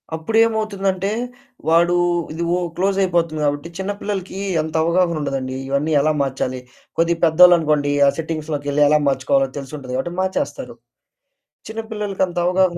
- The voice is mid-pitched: Yes, medium, 170 Hz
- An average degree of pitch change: Yes, average, 4.6 semitones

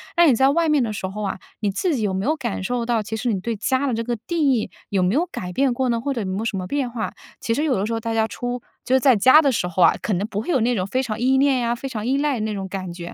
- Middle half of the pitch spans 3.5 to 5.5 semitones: Yes, average, 4.3 semitones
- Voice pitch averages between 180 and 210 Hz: No, high, 235 Hz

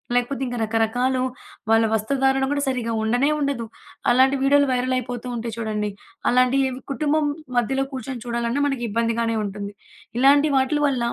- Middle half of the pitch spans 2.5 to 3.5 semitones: Yes, average, 2.8 semitones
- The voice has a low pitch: No, very high, 250 Hz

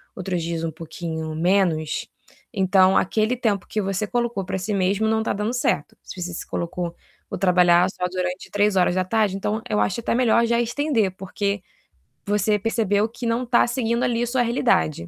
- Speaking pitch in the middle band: No, high, 200 Hz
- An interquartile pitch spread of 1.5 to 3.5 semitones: No, average, 4.1 semitones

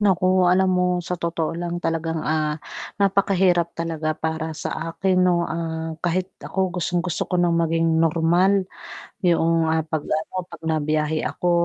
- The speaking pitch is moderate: Yes, medium, 170 Hz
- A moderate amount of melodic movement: No, narrow, 2.0 semitones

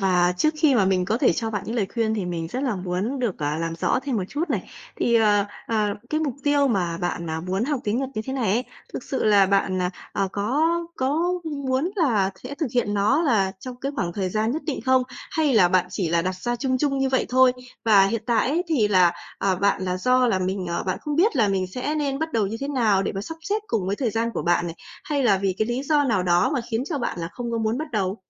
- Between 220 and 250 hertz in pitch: Yes, high, 225 Hz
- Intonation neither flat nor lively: No, wide, 6.0 semitones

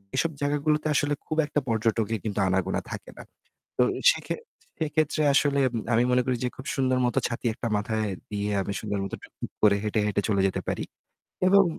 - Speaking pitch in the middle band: No, low, 115 Hz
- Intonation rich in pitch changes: Yes, wide, 5.7 semitones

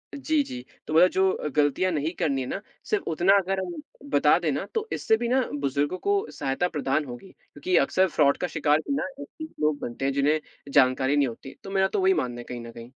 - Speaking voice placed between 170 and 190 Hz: No, medium, 155 Hz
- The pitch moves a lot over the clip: Yes, wide, 6.1 semitones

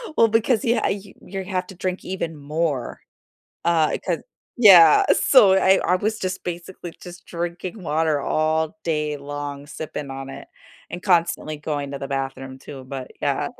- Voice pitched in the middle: Yes, medium, 165 Hz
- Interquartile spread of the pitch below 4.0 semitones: No, average, 4.3 semitones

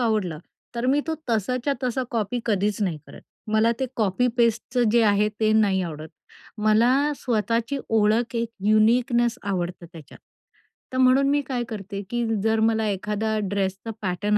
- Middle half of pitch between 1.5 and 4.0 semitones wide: Yes, average, 2.9 semitones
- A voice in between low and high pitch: No, high, 220 Hz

